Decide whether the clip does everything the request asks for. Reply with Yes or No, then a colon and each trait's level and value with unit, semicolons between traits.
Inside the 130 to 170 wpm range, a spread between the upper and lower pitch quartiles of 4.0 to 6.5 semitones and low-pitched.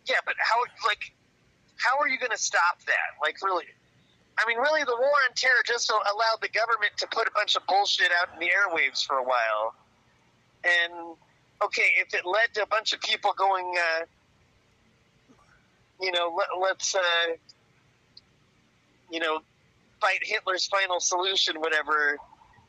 No: average, 160 wpm; wide, 5.4 semitones; medium, 175 Hz